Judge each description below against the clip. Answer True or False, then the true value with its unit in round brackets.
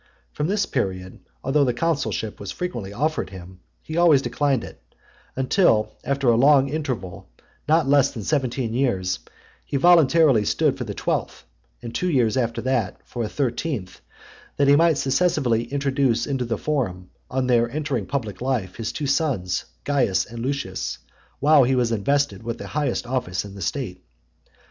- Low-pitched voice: True (130 Hz)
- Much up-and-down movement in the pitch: False (4.5 semitones)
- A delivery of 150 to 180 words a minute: True (165 wpm)